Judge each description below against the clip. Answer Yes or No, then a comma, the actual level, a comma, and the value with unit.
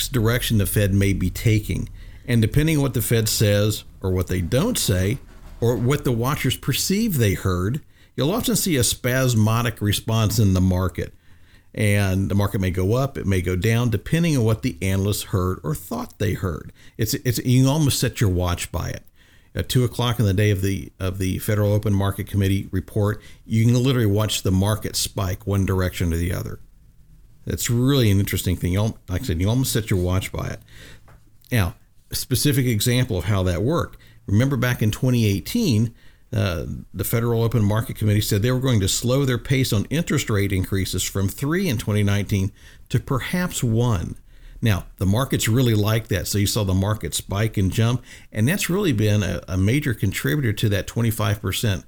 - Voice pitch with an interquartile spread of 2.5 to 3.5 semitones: No, average, 4.0 semitones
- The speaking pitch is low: Yes, low, 110 Hz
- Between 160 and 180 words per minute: No, average, 195 wpm